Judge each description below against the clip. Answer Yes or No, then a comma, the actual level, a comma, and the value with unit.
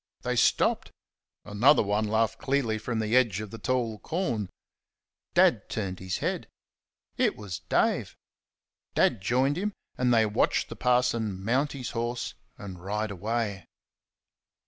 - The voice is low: Yes, low, 110 Hz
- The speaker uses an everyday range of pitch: Yes, average, 3.3 semitones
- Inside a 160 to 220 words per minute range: No, average, 140 wpm